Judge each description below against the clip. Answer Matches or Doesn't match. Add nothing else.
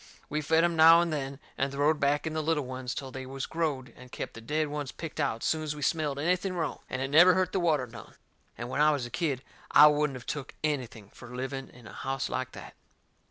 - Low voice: Doesn't match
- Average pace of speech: Doesn't match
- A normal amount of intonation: Matches